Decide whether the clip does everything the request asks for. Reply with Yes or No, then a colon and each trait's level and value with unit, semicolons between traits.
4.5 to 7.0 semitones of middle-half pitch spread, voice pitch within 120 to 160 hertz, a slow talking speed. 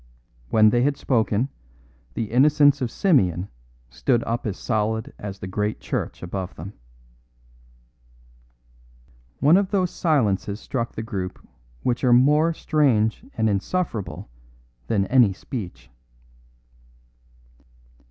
No: wide, 5.6 semitones; low, 110 Hz; slow, 115 wpm